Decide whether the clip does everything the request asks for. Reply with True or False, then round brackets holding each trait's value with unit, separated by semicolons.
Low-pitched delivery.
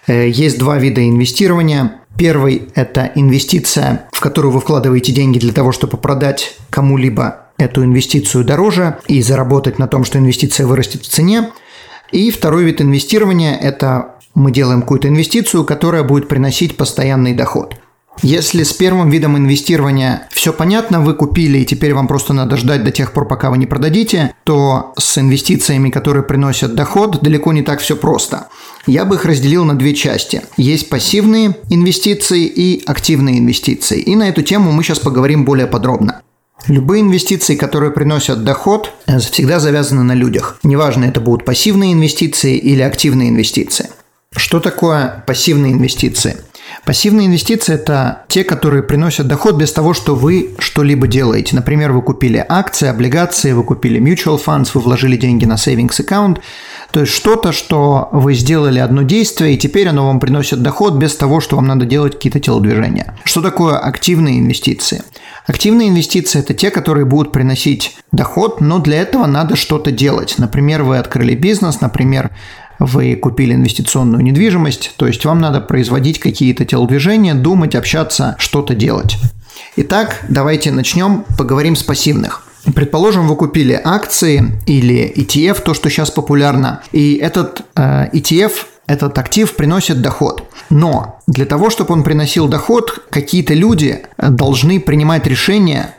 False (145 Hz)